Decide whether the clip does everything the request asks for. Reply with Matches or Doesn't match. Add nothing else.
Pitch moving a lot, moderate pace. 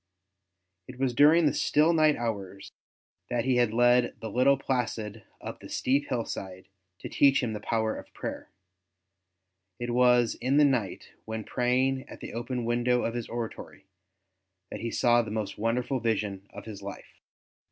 Doesn't match